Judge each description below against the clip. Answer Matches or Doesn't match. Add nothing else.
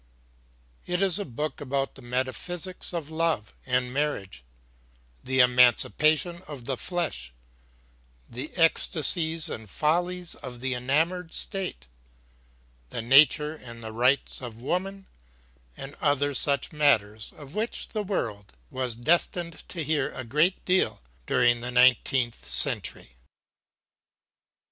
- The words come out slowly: Matches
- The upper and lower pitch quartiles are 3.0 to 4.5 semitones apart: Doesn't match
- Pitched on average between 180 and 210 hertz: Doesn't match